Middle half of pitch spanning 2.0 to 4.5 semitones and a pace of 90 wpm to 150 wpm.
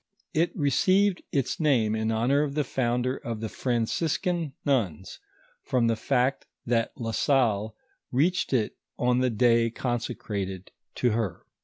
Yes: average, 3.8 semitones; average, 140 wpm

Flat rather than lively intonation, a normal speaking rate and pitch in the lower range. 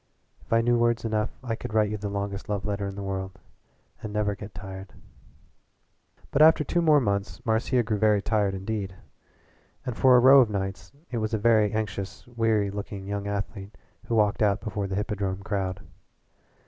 Yes: narrow, 2.2 semitones; average, 185 wpm; low, 105 Hz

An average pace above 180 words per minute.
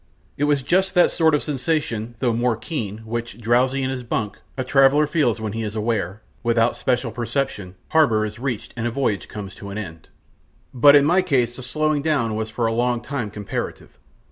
Yes: average, 200 wpm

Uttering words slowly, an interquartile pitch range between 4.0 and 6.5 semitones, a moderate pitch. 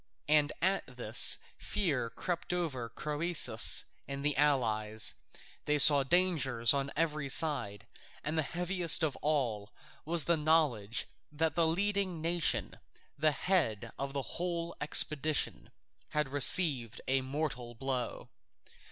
Yes: slow, 120 wpm; average, 4.3 semitones; medium, 150 Hz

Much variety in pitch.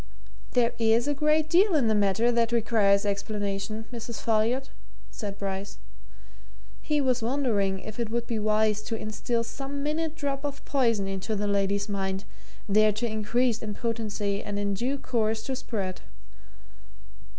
No: average, 3.5 semitones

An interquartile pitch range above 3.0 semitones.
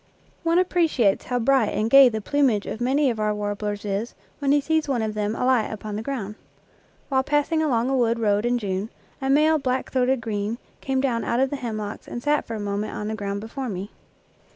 Yes: average, 4.3 semitones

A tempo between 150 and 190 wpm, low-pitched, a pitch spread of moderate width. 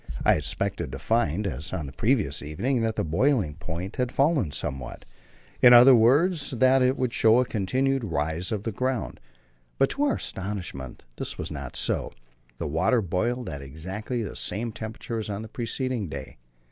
No: average, 180 wpm; low, 110 Hz; wide, 7.3 semitones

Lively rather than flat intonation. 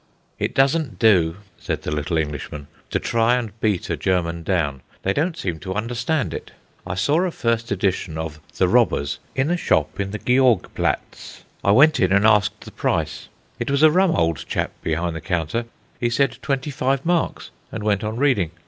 Yes: wide, 8.0 semitones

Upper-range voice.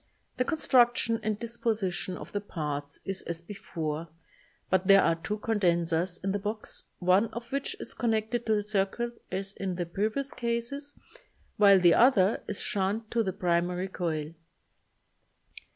Yes: high, 200 Hz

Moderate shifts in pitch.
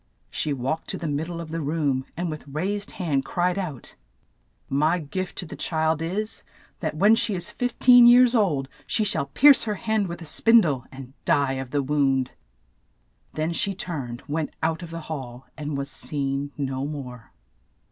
Yes: average, 4.7 semitones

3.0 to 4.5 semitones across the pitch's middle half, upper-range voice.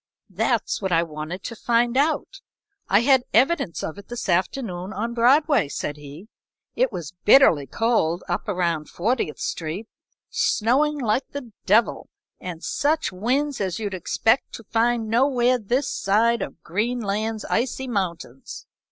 No: wide, 5.6 semitones; high, 225 Hz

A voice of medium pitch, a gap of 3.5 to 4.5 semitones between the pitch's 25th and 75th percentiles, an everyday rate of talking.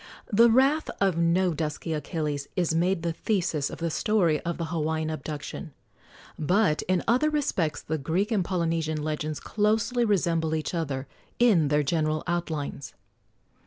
Yes: medium, 165 Hz; average, 4.0 semitones; average, 150 wpm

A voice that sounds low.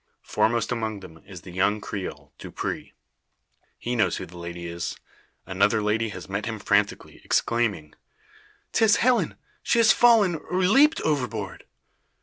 Yes: low, 110 Hz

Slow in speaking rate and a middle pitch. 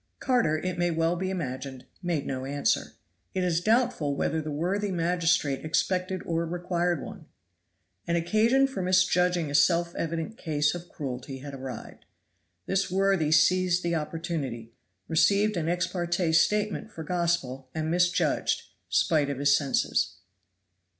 No: average, 145 wpm; medium, 170 Hz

